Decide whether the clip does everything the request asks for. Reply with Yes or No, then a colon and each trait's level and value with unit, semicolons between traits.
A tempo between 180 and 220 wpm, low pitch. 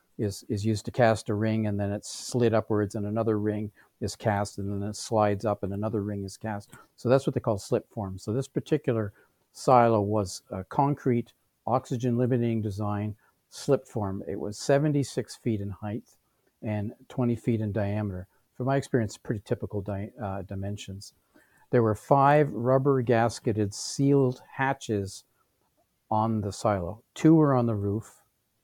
No: average, 170 wpm; low, 110 Hz